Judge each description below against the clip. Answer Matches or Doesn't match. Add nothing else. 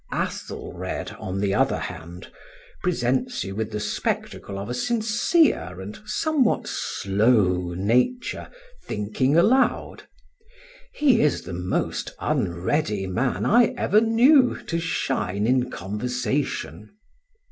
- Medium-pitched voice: Doesn't match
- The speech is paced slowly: Matches